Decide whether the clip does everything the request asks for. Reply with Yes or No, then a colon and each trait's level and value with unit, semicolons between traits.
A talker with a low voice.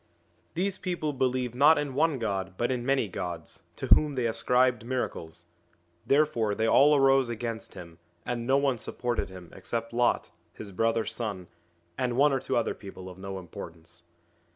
Yes: low, 120 Hz